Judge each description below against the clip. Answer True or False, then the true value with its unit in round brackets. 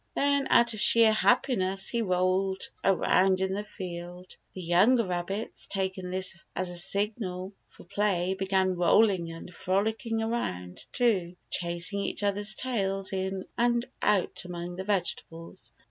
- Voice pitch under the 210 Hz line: True (190 Hz)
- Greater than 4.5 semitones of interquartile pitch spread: False (2.8 semitones)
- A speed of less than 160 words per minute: True (140 wpm)